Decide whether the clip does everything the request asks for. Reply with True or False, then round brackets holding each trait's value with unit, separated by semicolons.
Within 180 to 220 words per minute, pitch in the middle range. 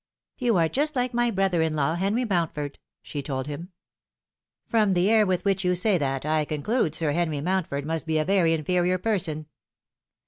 True (195 wpm; 175 Hz)